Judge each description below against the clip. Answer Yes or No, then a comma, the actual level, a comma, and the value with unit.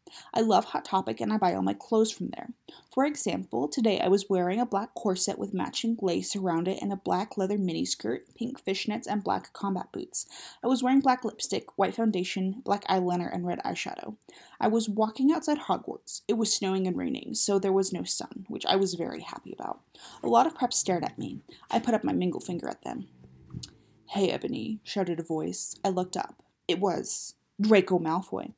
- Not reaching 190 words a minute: No, fast, 205 wpm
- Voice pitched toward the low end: No, high, 200 Hz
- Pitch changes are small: No, average, 3.7 semitones